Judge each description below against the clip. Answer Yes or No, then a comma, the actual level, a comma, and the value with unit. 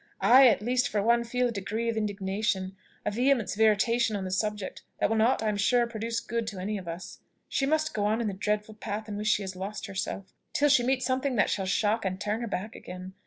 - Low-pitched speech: No, high, 215 Hz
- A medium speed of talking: No, fast, 250 wpm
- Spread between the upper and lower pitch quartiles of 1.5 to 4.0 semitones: Yes, average, 2.8 semitones